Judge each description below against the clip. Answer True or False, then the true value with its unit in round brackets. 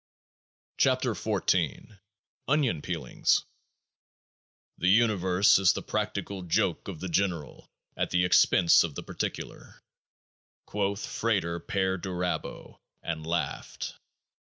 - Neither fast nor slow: False (105 wpm)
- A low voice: True (95 Hz)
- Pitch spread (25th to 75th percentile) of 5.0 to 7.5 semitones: False (2.9 semitones)